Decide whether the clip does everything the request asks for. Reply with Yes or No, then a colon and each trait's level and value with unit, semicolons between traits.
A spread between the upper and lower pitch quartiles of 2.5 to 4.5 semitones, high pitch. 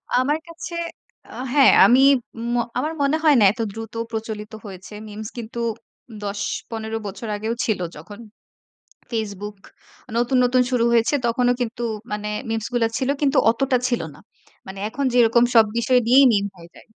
Yes: average, 3.1 semitones; high, 230 Hz